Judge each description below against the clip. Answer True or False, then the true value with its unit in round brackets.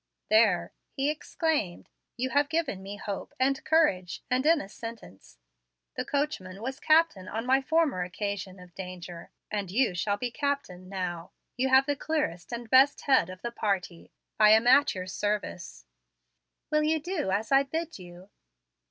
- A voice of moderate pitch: False (225 Hz)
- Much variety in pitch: True (7.3 semitones)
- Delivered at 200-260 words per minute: False (165 wpm)